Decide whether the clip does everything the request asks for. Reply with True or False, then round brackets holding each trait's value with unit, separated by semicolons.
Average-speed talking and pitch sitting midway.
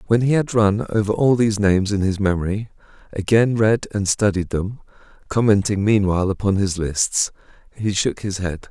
False (170 wpm; 100 Hz)